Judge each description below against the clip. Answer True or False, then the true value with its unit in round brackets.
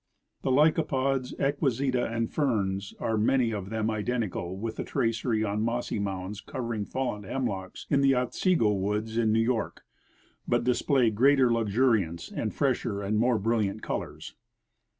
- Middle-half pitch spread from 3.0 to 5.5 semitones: True (3.5 semitones)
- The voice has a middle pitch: False (115 Hz)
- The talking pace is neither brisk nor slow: True (150 wpm)